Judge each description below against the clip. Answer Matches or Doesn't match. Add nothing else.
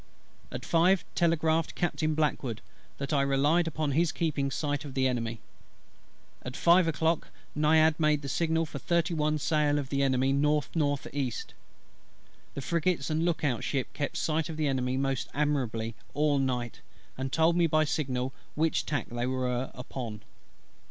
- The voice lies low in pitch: Doesn't match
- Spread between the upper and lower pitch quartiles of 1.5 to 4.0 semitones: Matches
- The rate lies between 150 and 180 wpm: Matches